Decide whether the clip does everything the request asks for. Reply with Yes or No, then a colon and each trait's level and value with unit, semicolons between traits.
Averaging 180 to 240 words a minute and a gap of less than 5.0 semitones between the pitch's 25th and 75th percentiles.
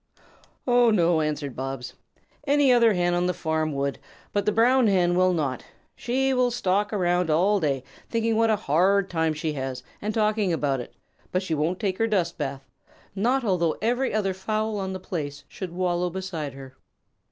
No: average, 185 wpm; wide, 5.5 semitones